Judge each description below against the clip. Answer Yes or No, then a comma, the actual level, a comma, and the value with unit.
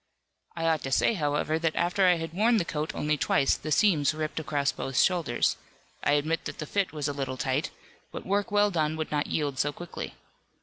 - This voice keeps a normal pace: No, fast, 215 wpm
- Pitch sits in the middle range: Yes, medium, 155 Hz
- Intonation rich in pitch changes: No, average, 3.1 semitones